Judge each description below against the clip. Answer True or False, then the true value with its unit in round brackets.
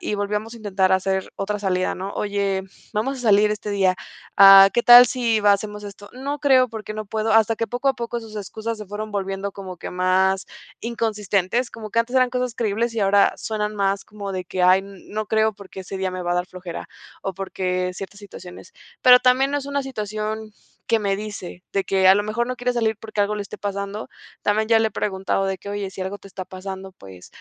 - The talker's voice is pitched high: True (205 Hz)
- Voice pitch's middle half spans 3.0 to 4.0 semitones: False (2.6 semitones)